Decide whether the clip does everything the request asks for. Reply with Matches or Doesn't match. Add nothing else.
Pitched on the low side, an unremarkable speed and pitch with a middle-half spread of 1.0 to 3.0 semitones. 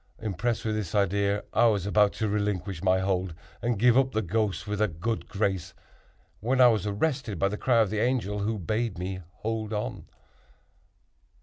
Matches